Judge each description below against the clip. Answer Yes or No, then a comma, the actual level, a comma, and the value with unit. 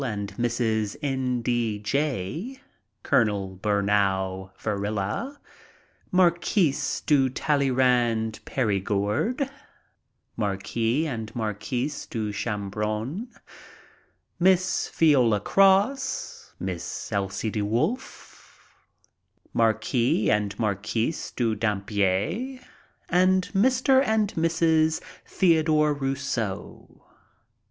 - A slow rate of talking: Yes, slow, 75 wpm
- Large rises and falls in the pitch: Yes, wide, 7.5 semitones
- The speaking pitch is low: Yes, low, 120 Hz